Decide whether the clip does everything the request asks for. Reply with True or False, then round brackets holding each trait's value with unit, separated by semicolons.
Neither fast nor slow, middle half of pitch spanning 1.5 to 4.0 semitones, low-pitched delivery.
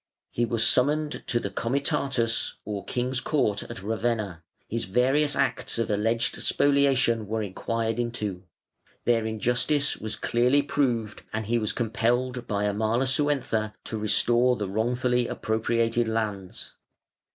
False (130 wpm; 2.6 semitones; 115 Hz)